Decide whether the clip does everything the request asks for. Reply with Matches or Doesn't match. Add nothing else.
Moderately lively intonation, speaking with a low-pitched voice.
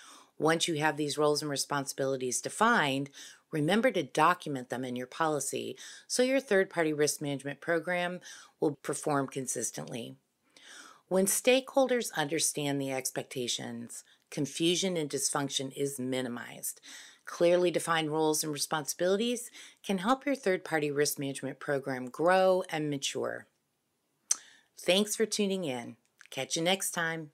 Doesn't match